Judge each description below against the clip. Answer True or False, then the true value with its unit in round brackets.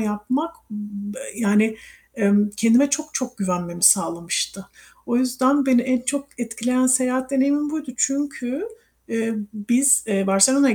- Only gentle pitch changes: False (4.5 semitones)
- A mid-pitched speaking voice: False (245 Hz)